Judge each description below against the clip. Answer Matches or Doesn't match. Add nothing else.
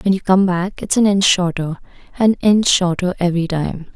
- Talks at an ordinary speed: Matches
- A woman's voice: Matches